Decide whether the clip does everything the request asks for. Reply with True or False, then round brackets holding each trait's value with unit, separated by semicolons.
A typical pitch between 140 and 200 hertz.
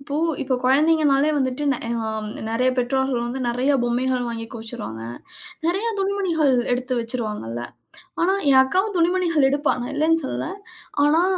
False (270 Hz)